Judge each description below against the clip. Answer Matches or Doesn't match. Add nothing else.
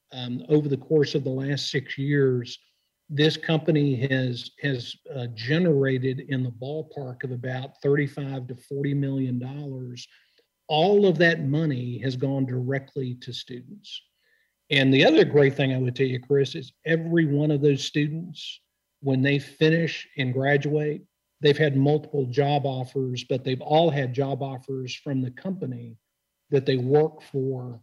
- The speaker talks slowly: Doesn't match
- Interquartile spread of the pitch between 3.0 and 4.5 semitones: Doesn't match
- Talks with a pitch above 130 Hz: Matches